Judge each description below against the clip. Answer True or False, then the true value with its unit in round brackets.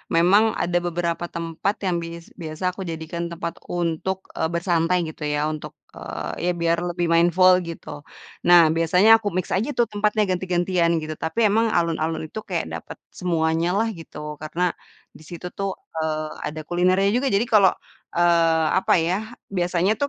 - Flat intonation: True (2.0 semitones)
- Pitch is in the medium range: True (175 Hz)